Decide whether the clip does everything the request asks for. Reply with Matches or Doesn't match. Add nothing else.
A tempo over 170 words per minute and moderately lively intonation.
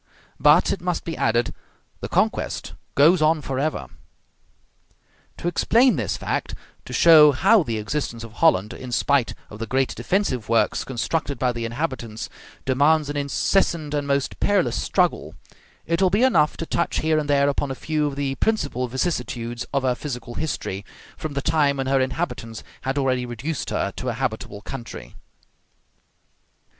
Doesn't match